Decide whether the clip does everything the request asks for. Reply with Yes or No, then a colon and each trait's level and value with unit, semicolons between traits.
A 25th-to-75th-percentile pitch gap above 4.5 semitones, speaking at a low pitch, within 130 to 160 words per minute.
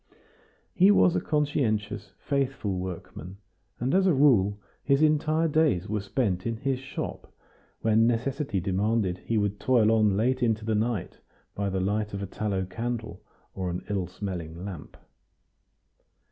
Yes: average, 5.2 semitones; low, 110 Hz; average, 150 wpm